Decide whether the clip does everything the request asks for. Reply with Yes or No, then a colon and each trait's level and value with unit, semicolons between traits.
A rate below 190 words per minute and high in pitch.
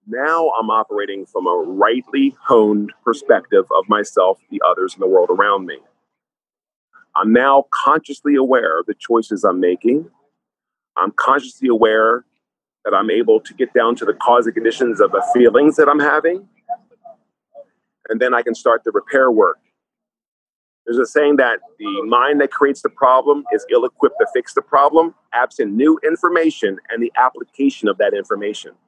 Yes: average, 165 wpm; high, 200 Hz